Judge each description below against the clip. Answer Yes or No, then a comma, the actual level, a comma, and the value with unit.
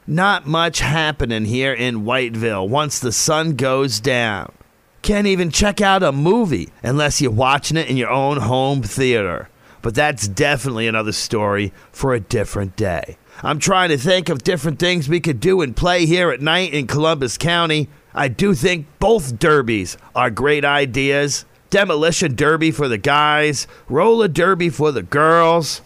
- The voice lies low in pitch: No, medium, 150 Hz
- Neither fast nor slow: Yes, average, 165 wpm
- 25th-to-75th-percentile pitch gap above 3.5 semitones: Yes, average, 5.0 semitones